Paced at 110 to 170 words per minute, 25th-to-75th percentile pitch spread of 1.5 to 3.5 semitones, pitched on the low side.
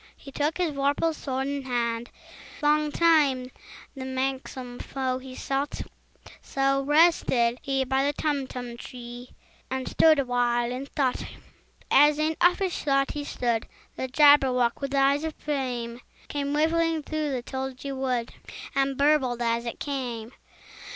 No: average, 145 wpm; average, 2.7 semitones; very high, 270 Hz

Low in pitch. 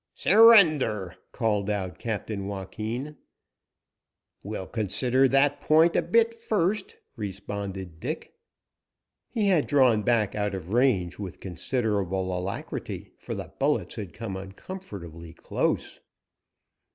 Yes: low, 105 Hz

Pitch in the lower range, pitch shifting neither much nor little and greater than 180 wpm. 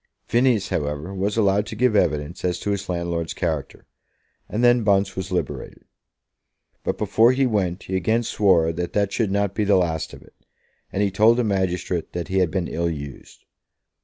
Yes: very low, 95 Hz; average, 3.3 semitones; average, 190 wpm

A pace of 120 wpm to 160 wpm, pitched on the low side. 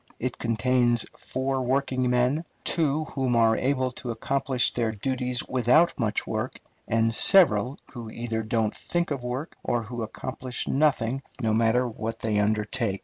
Yes: average, 150 wpm; low, 125 Hz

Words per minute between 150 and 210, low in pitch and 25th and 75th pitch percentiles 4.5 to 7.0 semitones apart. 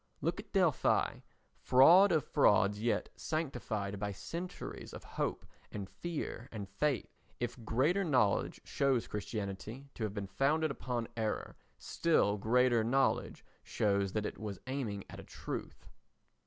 No: slow, 135 wpm; low, 115 Hz; average, 5.2 semitones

